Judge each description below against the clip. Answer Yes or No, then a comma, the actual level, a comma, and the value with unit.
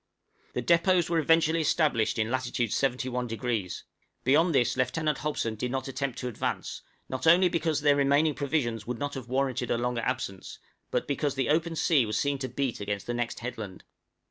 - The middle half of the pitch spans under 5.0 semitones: Yes, average, 4.1 semitones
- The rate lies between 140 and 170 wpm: No, average, 185 wpm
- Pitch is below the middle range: Yes, low, 130 Hz